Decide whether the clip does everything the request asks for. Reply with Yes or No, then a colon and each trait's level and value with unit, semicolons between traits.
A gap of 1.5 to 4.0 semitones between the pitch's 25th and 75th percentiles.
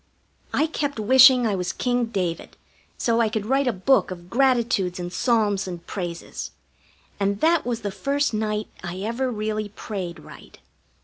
No: average, 4.6 semitones